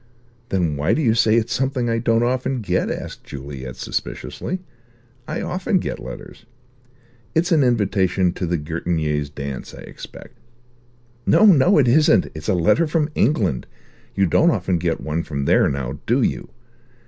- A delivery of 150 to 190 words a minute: Yes, average, 160 wpm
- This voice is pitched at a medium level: No, low, 100 Hz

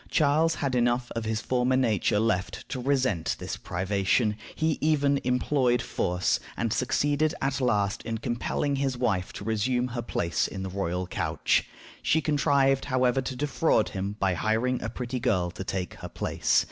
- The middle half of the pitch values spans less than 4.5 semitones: No, average, 4.8 semitones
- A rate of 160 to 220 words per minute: Yes, average, 170 wpm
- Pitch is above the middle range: No, low, 125 Hz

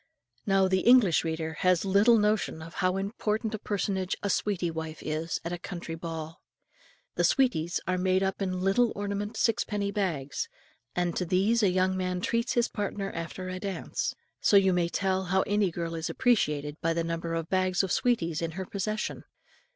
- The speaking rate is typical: Yes, average, 180 wpm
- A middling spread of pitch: Yes, average, 3.3 semitones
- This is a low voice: No, medium, 185 Hz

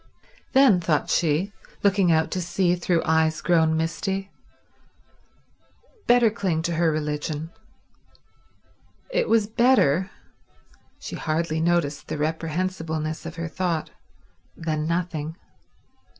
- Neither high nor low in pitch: Yes, medium, 165 Hz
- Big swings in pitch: No, average, 2.9 semitones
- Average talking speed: No, slow, 100 wpm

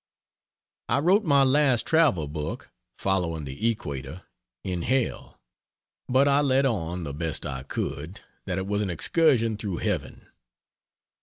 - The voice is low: Yes, low, 100 Hz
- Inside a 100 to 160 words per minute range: Yes, average, 140 wpm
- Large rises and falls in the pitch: Yes, wide, 8.7 semitones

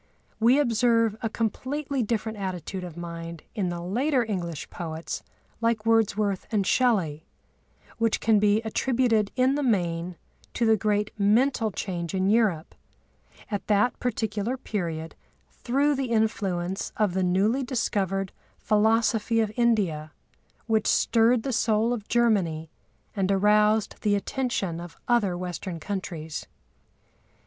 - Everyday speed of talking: No, slow, 130 wpm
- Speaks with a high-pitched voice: Yes, high, 210 Hz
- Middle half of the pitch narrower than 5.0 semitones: Yes, average, 4.0 semitones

